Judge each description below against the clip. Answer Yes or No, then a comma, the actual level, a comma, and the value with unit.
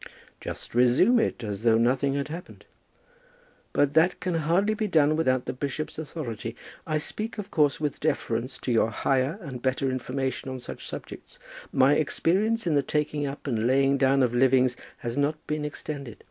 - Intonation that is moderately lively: Yes, average, 3.3 semitones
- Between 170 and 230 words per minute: Yes, average, 175 wpm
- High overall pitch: No, medium, 140 Hz